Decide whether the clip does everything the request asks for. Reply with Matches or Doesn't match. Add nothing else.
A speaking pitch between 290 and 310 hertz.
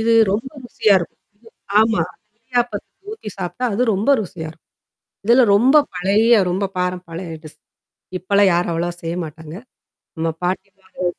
Doesn't match